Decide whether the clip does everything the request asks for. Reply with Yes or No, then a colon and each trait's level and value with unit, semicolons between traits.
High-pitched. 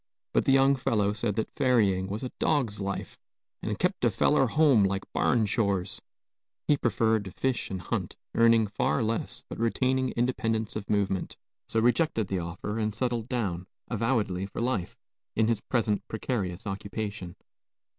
No: low, 110 Hz